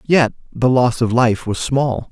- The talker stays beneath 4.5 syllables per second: Yes, 3.9 syllables/s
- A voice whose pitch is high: No, low, 120 Hz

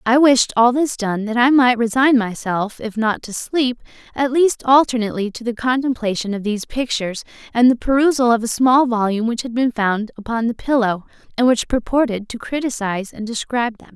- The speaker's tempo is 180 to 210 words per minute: Yes, average, 195 wpm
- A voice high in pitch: Yes, high, 235 Hz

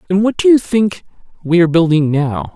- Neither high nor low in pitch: Yes, medium, 180 Hz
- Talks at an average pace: No, fast, 210 wpm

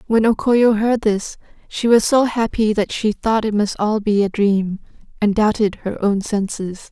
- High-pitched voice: Yes, high, 210 Hz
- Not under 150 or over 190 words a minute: No, average, 200 wpm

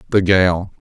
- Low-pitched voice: Yes, very low, 90 Hz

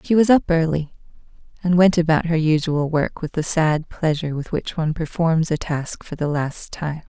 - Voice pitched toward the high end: No, medium, 160 Hz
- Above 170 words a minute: Yes, average, 200 wpm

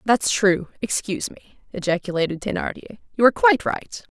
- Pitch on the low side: No, high, 205 Hz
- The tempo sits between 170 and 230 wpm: No, average, 145 wpm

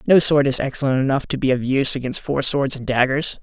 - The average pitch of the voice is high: No, low, 135 Hz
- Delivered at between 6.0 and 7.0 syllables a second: Yes, 6.1 syllables/s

